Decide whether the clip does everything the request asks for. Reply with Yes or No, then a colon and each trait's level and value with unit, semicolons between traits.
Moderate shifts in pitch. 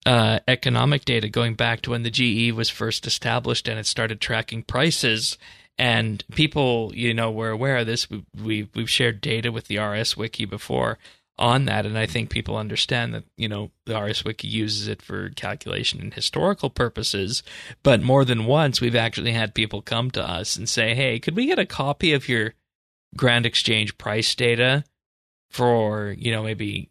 No: narrow, 2.1 semitones